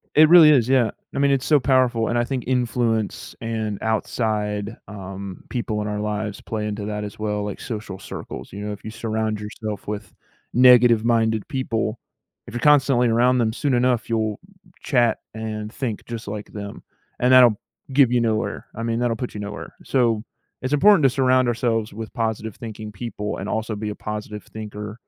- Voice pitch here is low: Yes, low, 110 Hz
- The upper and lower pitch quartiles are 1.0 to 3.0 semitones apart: Yes, narrow, 2.6 semitones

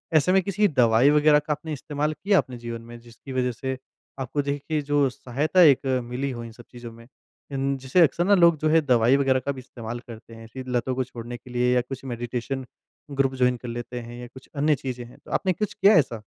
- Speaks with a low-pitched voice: Yes, low, 130 Hz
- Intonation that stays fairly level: No, average, 3.5 semitones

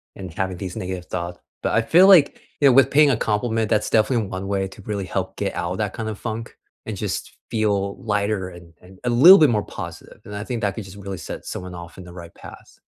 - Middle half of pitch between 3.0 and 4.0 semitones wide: Yes, average, 3.4 semitones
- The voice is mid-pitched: No, low, 105 Hz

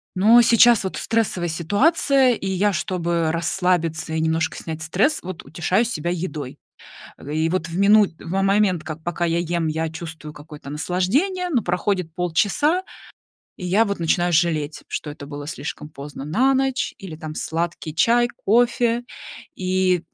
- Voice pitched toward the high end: No, medium, 175 Hz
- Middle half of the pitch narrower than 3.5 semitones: No, average, 4.4 semitones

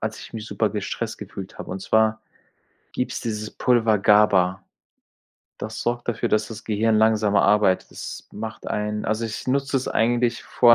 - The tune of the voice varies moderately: No, narrow, 1.6 semitones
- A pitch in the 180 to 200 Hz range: No, low, 110 Hz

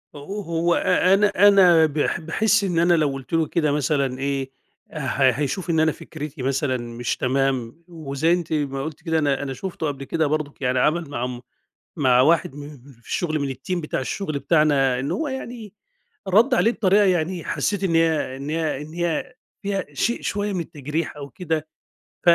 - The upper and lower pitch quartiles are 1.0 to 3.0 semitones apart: No, average, 4.2 semitones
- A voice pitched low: No, medium, 155 Hz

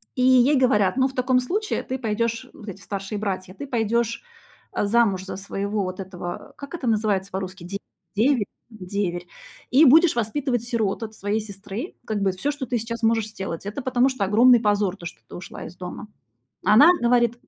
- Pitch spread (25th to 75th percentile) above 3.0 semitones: Yes, average, 4.1 semitones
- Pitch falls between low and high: No, high, 220 Hz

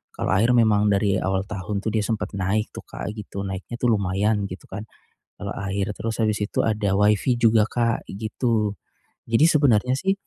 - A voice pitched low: Yes, low, 105 Hz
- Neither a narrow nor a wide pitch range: No, narrow, 2.3 semitones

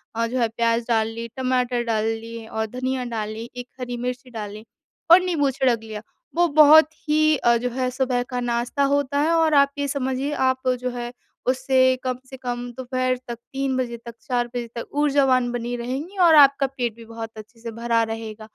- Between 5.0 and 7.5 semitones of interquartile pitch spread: No, narrow, 2.6 semitones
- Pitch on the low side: No, very high, 250 Hz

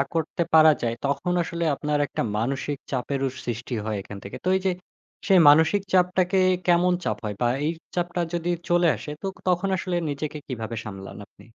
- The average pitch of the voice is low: No, medium, 155 Hz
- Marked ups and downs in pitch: Yes, wide, 5.9 semitones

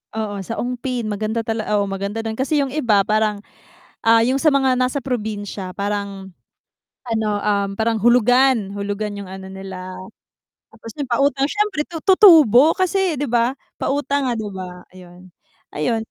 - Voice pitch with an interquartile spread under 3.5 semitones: No, average, 4.7 semitones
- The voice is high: Yes, high, 225 Hz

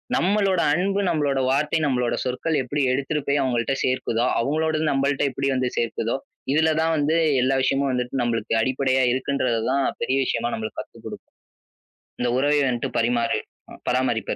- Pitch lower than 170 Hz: Yes, low, 135 Hz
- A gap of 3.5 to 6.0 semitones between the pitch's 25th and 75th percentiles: No, average, 3.0 semitones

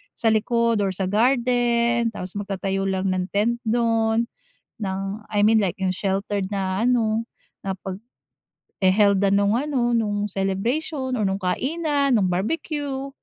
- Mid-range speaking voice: No, high, 215 Hz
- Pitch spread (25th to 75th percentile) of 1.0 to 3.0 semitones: No, average, 3.6 semitones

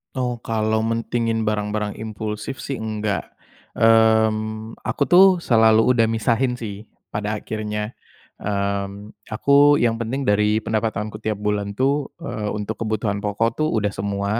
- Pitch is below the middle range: Yes, low, 110 Hz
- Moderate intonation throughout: No, narrow, 1.5 semitones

